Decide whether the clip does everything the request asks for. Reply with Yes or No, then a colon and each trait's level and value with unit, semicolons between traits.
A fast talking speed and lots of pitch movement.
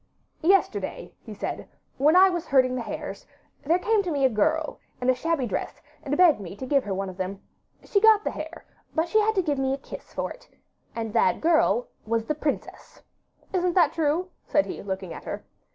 Yes: fast, 215 wpm; wide, 6.1 semitones